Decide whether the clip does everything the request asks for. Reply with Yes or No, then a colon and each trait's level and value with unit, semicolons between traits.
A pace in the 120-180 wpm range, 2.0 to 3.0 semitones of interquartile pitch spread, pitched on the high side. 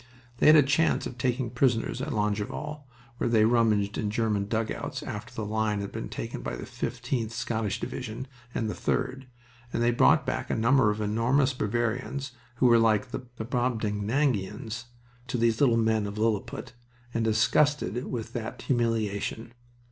No: average, 165 wpm; average, 2.7 semitones; low, 115 Hz